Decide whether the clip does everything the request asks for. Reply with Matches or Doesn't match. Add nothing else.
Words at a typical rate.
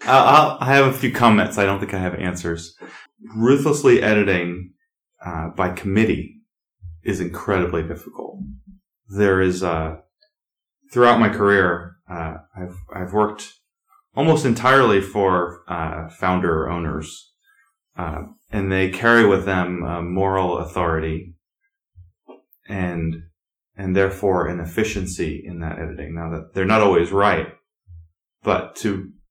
Doesn't match